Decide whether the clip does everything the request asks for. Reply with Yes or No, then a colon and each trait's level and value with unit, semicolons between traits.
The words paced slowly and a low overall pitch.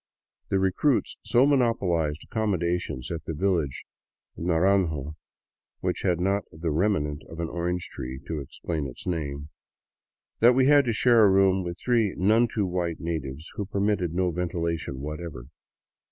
No: average, 160 wpm; very low, 90 Hz